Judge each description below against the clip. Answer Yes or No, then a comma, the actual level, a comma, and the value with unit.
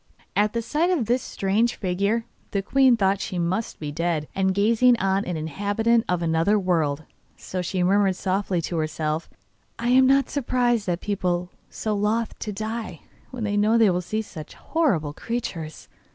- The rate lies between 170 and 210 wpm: Yes, average, 180 wpm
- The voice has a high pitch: Yes, high, 200 Hz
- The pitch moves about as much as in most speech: Yes, average, 4.6 semitones